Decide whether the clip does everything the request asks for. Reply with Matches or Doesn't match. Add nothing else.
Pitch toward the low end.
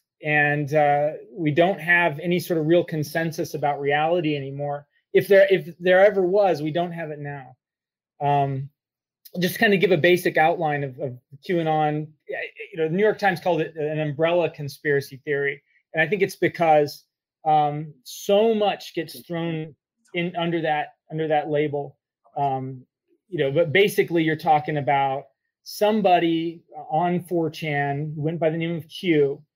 Doesn't match